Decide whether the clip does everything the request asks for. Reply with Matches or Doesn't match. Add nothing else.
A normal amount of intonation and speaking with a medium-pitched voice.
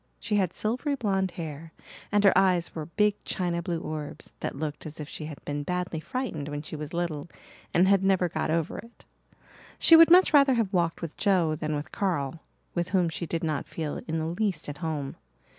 Matches